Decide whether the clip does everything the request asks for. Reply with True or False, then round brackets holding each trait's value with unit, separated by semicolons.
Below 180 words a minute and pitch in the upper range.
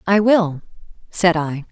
False (140 wpm; 180 Hz)